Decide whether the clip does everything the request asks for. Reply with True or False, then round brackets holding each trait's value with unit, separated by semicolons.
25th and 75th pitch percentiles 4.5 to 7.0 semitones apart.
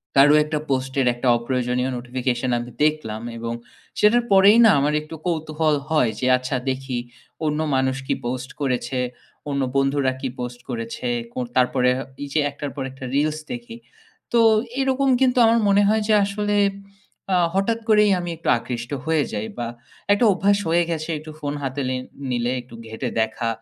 True (5.5 semitones)